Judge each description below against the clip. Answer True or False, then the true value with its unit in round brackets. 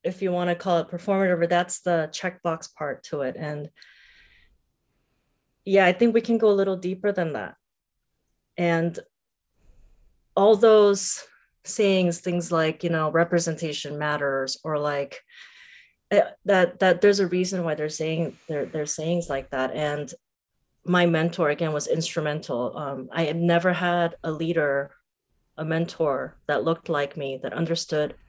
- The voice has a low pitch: False (170 Hz)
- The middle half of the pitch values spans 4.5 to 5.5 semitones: False (3.2 semitones)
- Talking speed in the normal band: True (155 wpm)